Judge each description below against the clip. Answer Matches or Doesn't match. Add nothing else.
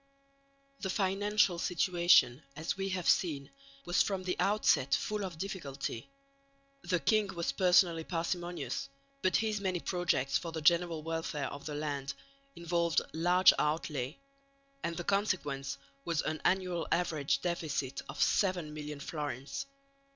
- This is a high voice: Doesn't match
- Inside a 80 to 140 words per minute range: Matches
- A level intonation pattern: Doesn't match